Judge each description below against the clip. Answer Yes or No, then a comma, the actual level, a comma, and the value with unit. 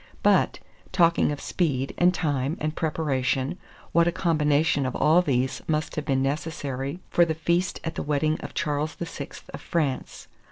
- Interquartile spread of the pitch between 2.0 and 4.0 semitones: Yes, average, 3.1 semitones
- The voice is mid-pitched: Yes, medium, 150 Hz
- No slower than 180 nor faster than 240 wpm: No, average, 165 wpm